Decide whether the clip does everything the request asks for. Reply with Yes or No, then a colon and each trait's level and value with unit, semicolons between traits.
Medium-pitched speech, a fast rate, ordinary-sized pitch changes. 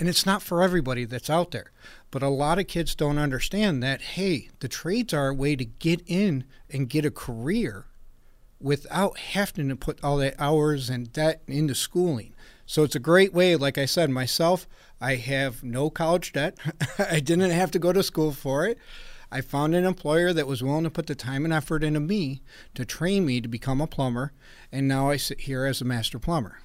Yes: medium, 150 Hz; fast, 210 wpm; average, 4.1 semitones